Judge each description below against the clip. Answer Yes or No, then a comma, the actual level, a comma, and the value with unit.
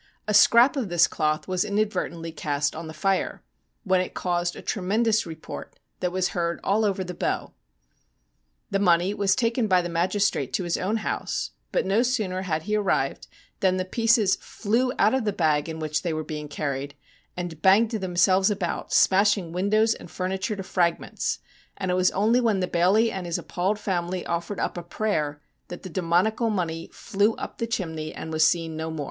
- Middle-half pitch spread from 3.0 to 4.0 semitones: Yes, average, 3.7 semitones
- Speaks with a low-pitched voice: No, medium, 185 Hz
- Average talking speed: Yes, average, 190 wpm